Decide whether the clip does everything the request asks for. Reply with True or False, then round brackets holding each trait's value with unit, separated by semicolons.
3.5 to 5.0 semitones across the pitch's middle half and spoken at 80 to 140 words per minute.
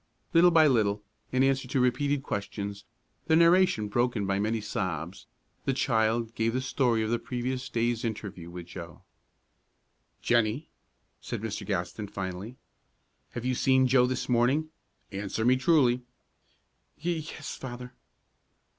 True (4.1 semitones; 135 wpm)